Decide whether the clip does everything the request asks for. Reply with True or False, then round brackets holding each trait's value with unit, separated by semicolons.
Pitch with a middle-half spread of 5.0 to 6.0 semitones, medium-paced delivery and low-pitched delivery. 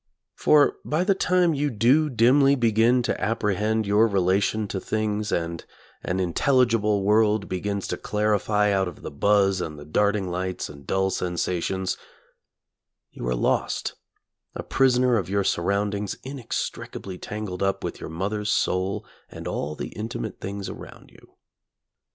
False (3.2 semitones; 145 wpm; 105 Hz)